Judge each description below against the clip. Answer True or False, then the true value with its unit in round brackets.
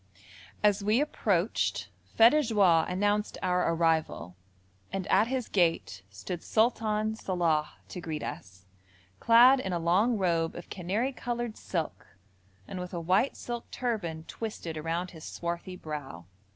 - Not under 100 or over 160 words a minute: True (140 wpm)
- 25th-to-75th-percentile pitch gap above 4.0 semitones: True (4.9 semitones)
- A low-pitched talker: False (185 Hz)